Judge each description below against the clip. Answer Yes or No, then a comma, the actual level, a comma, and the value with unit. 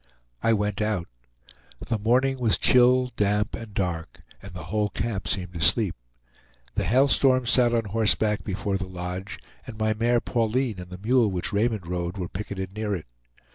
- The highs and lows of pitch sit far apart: No, average, 3.9 semitones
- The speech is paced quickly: No, average, 175 wpm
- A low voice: Yes, low, 105 Hz